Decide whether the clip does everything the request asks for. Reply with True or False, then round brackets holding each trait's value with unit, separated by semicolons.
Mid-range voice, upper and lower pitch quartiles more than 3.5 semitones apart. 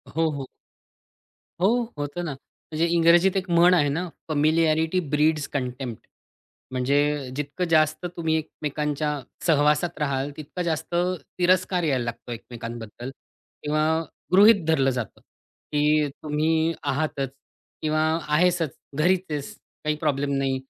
False (155 Hz; 2.8 semitones)